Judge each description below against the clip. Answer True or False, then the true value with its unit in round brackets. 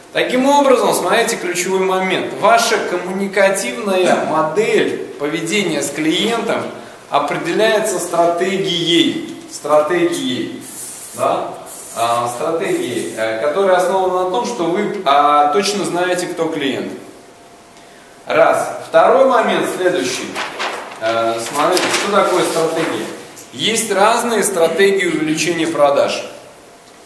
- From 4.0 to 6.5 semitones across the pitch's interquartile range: True (5.3 semitones)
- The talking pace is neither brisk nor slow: False (85 wpm)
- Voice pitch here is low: False (185 Hz)